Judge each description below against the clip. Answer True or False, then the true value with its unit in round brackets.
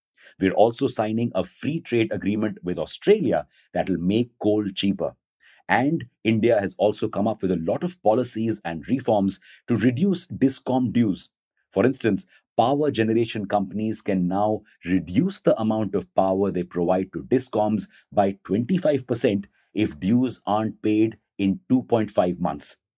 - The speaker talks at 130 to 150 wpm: True (145 wpm)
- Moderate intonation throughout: True (3.7 semitones)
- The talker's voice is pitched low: True (110 Hz)